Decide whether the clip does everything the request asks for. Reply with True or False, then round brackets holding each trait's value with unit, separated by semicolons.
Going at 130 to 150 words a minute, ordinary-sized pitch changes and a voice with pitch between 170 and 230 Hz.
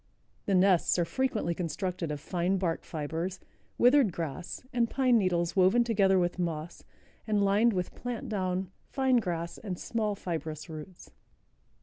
True (145 wpm; 4.1 semitones; 185 Hz)